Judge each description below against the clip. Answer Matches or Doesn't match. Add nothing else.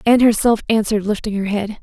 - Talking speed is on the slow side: Doesn't match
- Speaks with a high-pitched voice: Matches